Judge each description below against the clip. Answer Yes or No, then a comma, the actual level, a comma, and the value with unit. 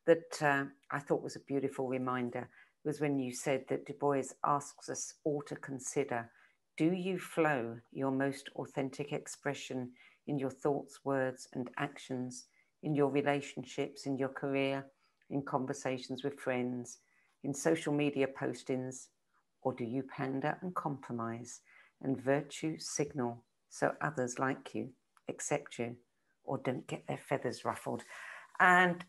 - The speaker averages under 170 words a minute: Yes, average, 140 wpm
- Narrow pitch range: Yes, narrow, 2.0 semitones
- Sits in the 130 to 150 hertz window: Yes, low, 135 Hz